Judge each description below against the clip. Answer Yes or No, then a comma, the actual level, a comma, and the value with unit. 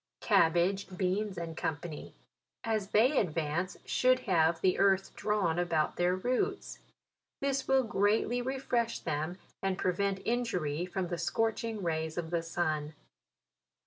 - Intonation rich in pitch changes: No, average, 5.0 semitones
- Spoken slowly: Yes, slow, 125 wpm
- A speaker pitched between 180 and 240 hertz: Yes, medium, 185 Hz